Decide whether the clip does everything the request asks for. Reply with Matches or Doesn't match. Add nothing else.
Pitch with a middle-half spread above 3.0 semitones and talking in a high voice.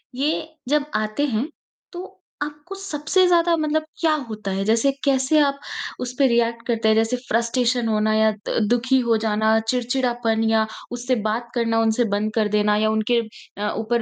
Matches